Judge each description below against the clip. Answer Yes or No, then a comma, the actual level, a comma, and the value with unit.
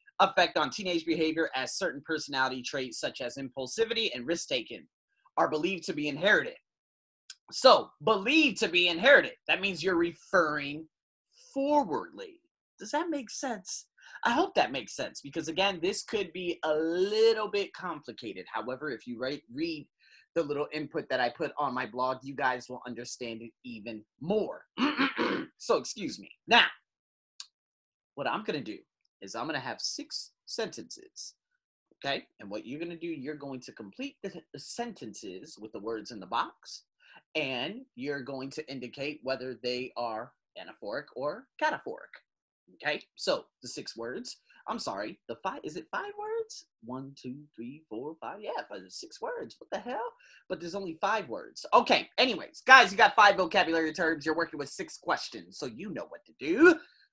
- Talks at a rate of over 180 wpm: No, average, 170 wpm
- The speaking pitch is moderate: Yes, medium, 175 Hz